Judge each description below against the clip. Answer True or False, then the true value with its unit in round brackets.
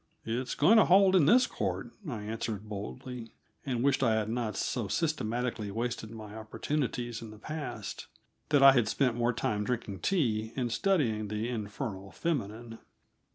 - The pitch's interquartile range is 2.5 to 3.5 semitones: False (4.0 semitones)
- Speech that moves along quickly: False (160 wpm)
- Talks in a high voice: False (115 Hz)